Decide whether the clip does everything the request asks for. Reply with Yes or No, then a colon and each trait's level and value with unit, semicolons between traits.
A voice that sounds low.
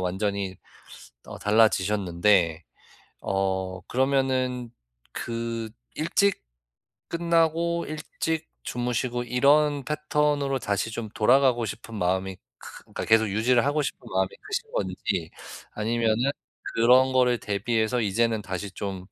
Yes: low, 115 Hz